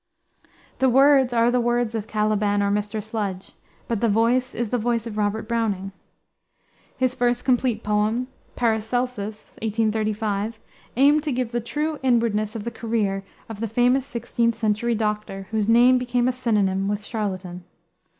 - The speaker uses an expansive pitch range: No, narrow, 2.5 semitones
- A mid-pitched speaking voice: No, high, 225 Hz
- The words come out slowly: No, average, 155 wpm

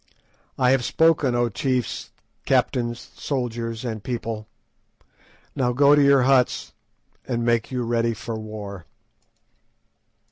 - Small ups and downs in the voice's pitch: Yes, narrow, 2.2 semitones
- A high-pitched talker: No, low, 120 Hz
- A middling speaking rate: No, slow, 115 wpm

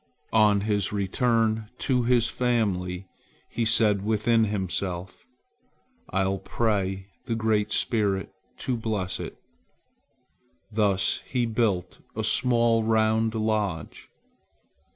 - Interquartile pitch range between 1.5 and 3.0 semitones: Yes, average, 2.7 semitones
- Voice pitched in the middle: No, low, 110 Hz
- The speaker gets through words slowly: Yes, slow, 100 wpm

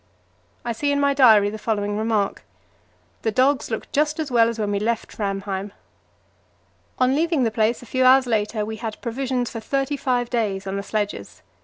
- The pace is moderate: Yes, average, 190 wpm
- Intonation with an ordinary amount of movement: Yes, average, 3.7 semitones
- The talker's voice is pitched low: No, high, 230 Hz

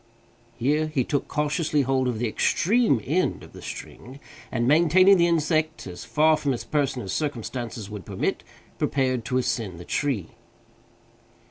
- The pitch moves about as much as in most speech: Yes, average, 4.6 semitones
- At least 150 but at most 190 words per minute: Yes, average, 155 wpm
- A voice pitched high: No, medium, 140 Hz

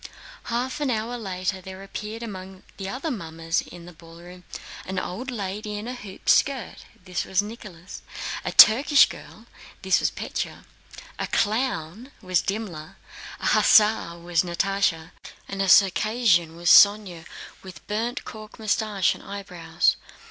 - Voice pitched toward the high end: Yes, high, 195 Hz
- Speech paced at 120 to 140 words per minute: Yes, slow, 135 wpm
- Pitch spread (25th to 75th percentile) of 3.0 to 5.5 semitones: Yes, average, 3.7 semitones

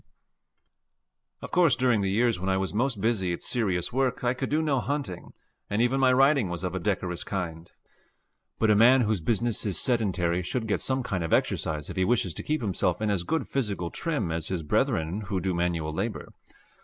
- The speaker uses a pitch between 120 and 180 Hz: No, low, 105 Hz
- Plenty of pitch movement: Yes, wide, 5.8 semitones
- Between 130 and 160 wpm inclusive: No, fast, 205 wpm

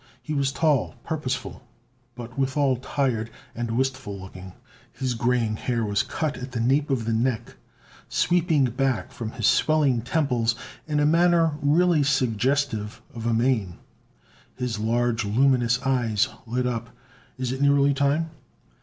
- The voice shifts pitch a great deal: No, average, 3.5 semitones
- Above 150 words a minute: No, average, 145 wpm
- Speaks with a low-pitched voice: Yes, low, 130 Hz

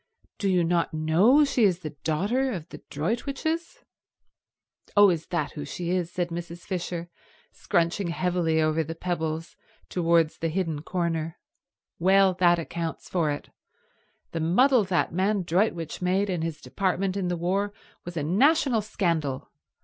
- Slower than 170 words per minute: Yes, average, 150 wpm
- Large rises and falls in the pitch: No, average, 3.1 semitones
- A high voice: No, medium, 175 Hz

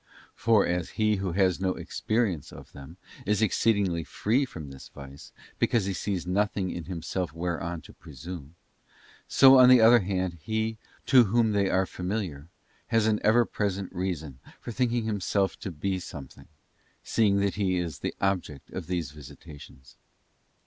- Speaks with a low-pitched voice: Yes, very low, 95 Hz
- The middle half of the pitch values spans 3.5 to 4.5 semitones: Yes, average, 4.1 semitones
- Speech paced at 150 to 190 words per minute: Yes, average, 160 wpm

